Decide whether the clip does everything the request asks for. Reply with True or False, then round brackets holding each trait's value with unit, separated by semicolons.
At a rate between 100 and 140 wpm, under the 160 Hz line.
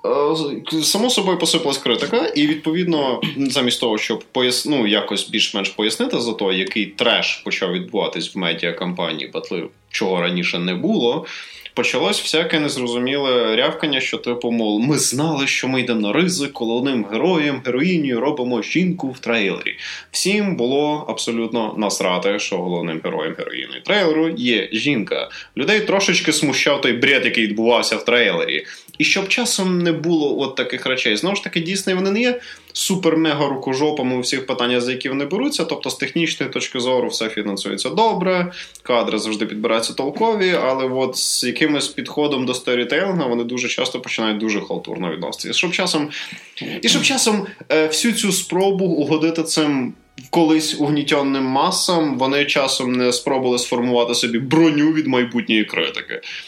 False (150 wpm; 140 Hz)